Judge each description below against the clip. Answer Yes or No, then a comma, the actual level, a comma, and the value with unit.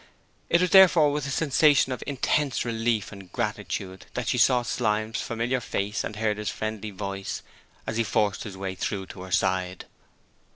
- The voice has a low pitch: Yes, low, 110 Hz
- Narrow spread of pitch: No, average, 4.7 semitones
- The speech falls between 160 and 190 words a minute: Yes, average, 175 wpm